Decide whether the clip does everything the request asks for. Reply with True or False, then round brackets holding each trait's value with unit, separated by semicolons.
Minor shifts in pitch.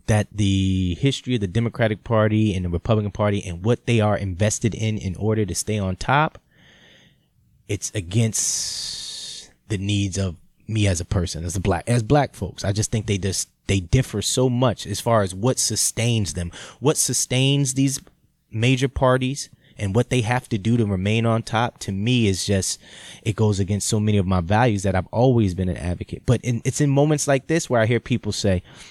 False (3.8 semitones)